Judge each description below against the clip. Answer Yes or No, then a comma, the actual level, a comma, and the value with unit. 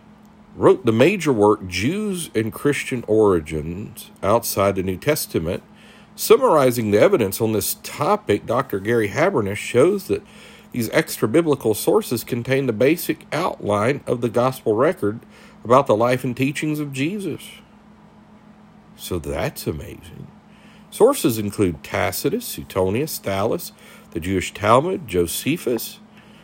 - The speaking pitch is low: Yes, low, 125 Hz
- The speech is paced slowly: Yes, slow, 125 wpm